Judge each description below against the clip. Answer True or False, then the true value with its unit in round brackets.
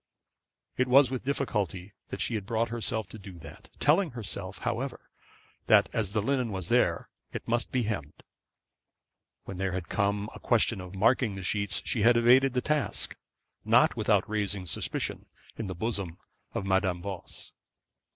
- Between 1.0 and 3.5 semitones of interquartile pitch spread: False (4.0 semitones)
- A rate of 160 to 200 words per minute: True (165 wpm)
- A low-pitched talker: True (105 Hz)